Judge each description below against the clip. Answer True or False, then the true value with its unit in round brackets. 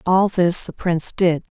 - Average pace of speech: True (190 wpm)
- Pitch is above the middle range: False (175 Hz)